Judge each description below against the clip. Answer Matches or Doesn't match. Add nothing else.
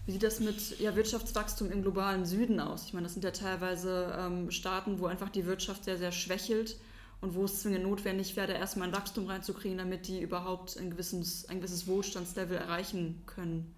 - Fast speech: Matches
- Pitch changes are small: Matches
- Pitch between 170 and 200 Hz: Matches